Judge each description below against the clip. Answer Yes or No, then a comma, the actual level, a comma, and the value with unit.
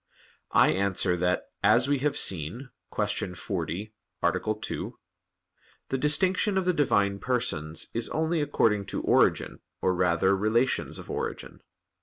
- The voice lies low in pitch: Yes, low, 110 Hz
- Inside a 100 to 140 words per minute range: Yes, slow, 135 wpm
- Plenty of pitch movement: Yes, wide, 6.8 semitones